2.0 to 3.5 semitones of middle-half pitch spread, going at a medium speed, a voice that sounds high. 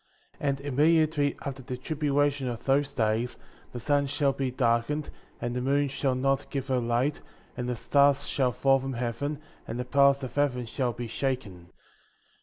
No: narrow, 2.5 semitones; average, 180 wpm; low, 135 Hz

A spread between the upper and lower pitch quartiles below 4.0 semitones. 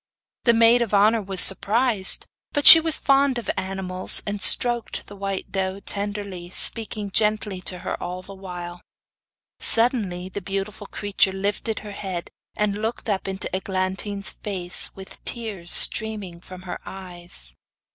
Yes: narrow, 2.4 semitones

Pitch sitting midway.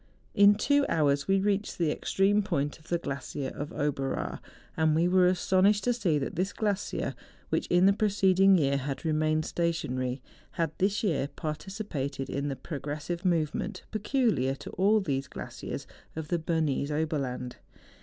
Yes: medium, 165 Hz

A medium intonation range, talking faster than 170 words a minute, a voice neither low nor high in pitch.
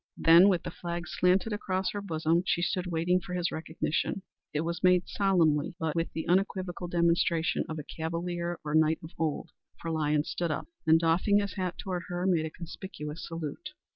No: narrow, 2.1 semitones; average, 190 wpm; medium, 170 Hz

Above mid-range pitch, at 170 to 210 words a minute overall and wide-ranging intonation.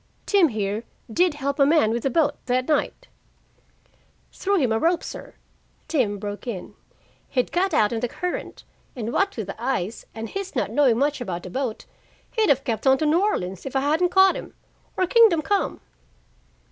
Yes: very high, 270 Hz; average, 195 wpm; wide, 7.6 semitones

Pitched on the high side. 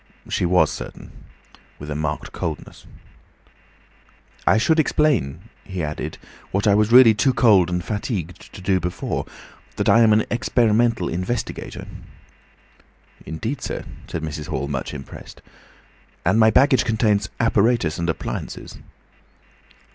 No: low, 100 Hz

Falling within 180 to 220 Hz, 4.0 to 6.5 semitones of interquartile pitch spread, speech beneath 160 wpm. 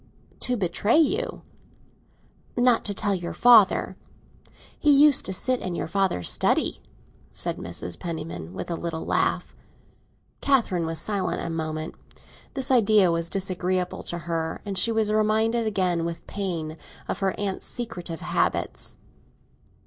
Yes: high, 190 Hz; average, 4.8 semitones; average, 140 wpm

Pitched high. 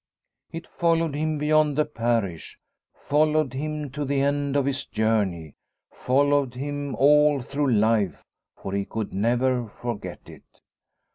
No: medium, 140 Hz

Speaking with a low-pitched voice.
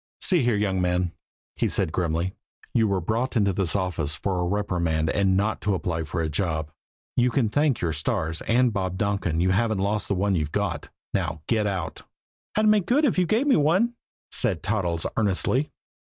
Yes: low, 100 Hz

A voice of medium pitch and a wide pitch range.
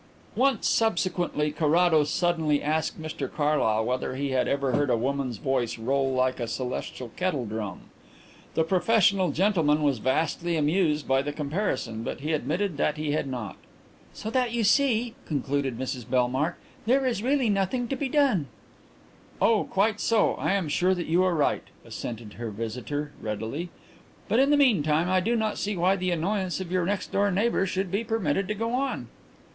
Yes: medium, 160 Hz; wide, 6.8 semitones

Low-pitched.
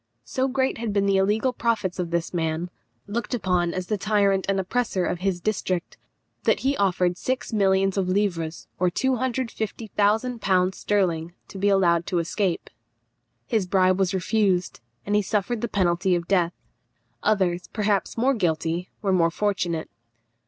No: high, 195 Hz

